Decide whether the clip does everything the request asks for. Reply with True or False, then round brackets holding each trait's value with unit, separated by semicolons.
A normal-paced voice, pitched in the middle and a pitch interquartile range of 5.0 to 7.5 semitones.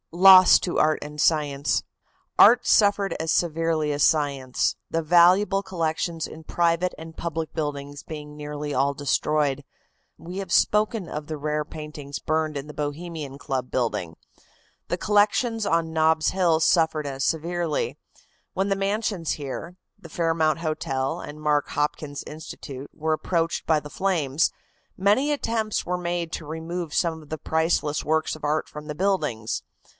False (150 wpm; 160 Hz; 2.8 semitones)